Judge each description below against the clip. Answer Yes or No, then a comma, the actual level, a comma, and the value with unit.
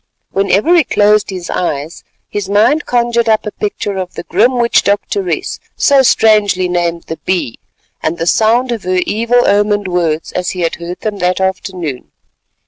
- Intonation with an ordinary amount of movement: Yes, average, 3.8 semitones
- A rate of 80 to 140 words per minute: No, average, 170 wpm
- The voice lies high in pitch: Yes, high, 200 Hz